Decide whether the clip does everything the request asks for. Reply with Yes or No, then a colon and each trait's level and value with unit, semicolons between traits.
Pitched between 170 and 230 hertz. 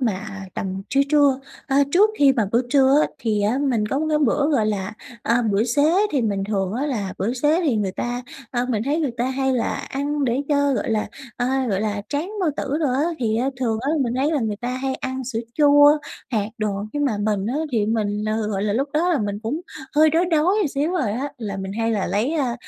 No: high, 245 Hz